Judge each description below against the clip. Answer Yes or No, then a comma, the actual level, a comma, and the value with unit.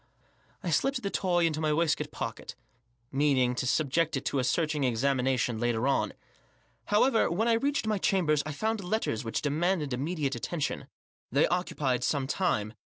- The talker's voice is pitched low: No, medium, 150 Hz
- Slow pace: No, average, 160 wpm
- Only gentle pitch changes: No, wide, 5.5 semitones